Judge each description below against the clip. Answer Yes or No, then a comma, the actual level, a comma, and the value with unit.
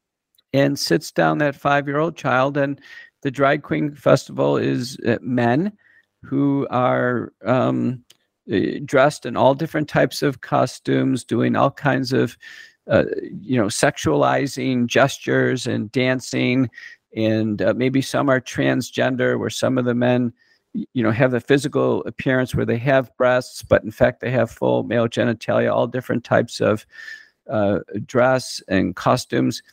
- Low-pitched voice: Yes, low, 130 Hz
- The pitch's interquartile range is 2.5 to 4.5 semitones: Yes, average, 3.7 semitones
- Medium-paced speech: Yes, average, 145 wpm